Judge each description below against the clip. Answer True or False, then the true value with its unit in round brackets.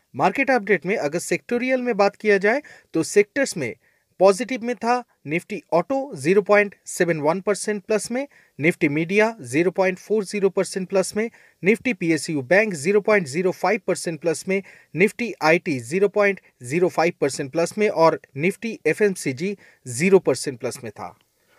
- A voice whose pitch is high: True (195 Hz)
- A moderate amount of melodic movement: True (4.1 semitones)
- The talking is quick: False (135 wpm)